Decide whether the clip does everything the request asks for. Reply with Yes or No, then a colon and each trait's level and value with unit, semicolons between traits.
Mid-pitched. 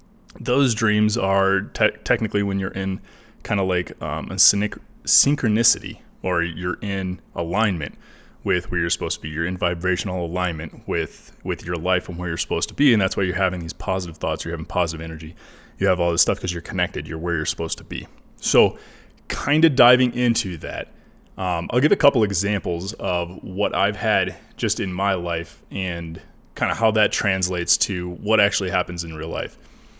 No: very low, 90 Hz